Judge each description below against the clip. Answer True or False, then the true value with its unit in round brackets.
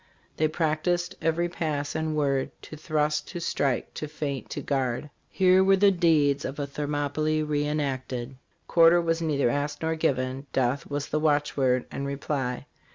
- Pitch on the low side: False (150 Hz)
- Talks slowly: False (170 wpm)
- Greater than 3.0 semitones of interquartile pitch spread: False (2.5 semitones)